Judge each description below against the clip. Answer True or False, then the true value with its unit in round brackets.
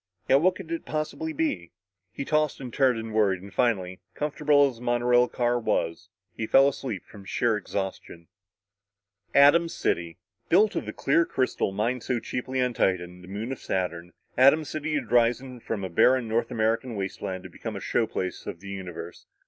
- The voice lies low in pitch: True (120 Hz)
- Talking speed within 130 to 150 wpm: False (180 wpm)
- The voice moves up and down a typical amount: False (5.9 semitones)